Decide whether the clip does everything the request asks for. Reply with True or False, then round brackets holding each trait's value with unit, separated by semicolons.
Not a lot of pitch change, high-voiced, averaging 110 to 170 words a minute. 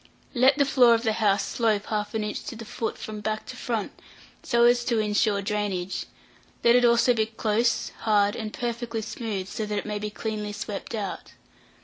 False (2.1 semitones; 220 Hz; 200 wpm)